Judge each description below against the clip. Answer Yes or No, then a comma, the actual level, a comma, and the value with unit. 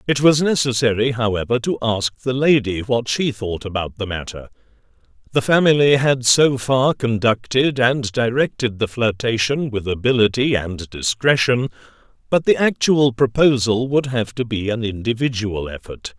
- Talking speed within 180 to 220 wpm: No, average, 145 wpm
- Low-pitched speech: Yes, low, 120 Hz